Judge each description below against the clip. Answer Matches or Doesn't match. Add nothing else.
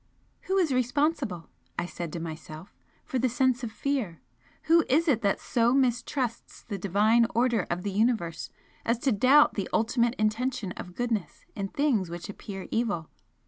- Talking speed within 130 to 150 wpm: Doesn't match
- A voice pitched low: Doesn't match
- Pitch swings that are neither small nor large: Matches